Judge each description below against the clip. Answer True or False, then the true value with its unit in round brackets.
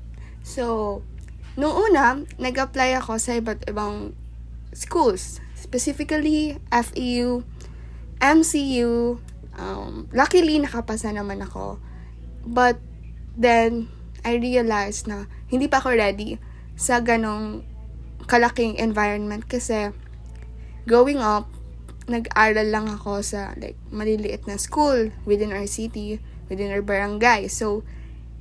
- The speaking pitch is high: True (220 Hz)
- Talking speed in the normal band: False (100 wpm)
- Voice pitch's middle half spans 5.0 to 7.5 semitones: False (3.4 semitones)